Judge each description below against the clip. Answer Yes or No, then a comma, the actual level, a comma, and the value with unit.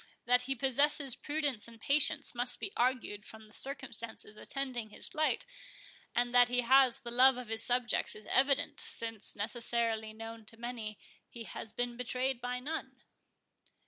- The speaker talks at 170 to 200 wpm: No, average, 160 wpm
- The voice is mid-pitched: No, high, 245 Hz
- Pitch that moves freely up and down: No, average, 2.7 semitones